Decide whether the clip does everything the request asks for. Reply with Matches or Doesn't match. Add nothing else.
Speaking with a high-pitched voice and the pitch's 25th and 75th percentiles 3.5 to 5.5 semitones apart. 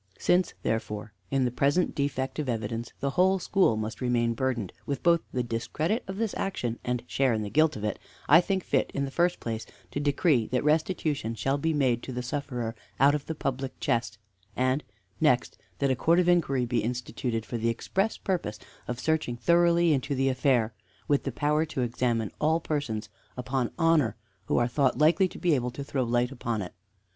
Doesn't match